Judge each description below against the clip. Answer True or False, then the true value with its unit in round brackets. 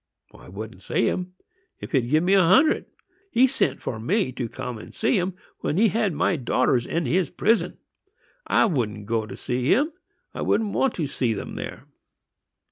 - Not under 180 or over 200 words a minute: True (185 wpm)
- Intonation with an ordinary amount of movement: False (8.8 semitones)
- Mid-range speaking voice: True (155 Hz)